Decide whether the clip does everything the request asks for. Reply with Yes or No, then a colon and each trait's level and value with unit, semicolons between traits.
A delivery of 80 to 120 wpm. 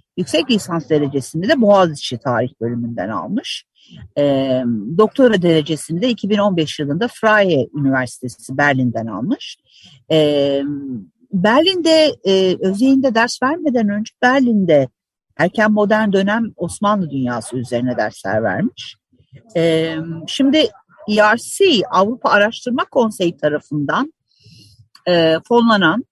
Yes: average, 100 wpm